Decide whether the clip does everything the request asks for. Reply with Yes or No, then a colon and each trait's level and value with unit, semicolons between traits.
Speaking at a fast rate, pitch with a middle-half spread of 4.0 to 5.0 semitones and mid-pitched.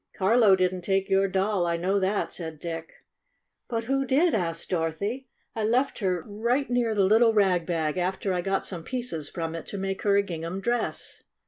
No: fast, 220 wpm; average, 4.4 semitones; high, 195 Hz